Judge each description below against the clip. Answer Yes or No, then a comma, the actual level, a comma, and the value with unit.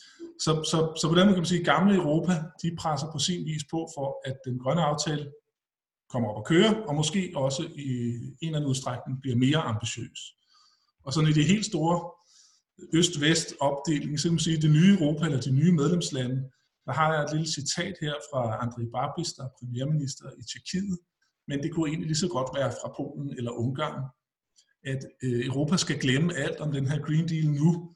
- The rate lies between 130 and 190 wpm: No, average, 200 wpm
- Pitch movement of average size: Yes, average, 4.0 semitones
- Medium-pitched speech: Yes, medium, 155 Hz